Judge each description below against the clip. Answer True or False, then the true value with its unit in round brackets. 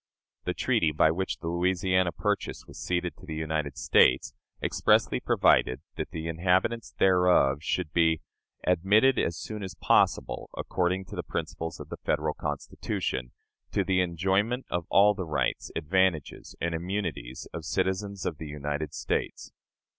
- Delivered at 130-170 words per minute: True (150 wpm)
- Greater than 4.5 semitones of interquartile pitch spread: False (3.1 semitones)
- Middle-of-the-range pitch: False (85 Hz)